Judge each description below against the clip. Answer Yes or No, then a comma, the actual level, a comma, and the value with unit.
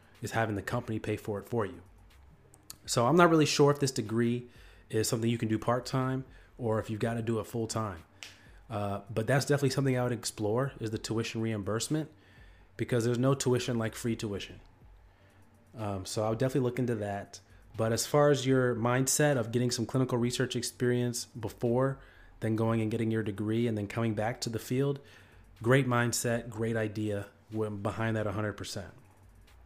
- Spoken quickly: No, average, 190 wpm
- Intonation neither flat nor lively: Yes, average, 3.0 semitones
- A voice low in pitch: Yes, low, 115 Hz